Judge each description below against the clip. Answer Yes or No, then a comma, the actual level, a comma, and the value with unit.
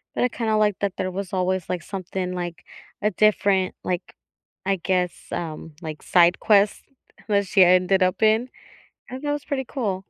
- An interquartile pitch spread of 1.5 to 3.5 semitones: Yes, average, 2.8 semitones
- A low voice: No, high, 190 Hz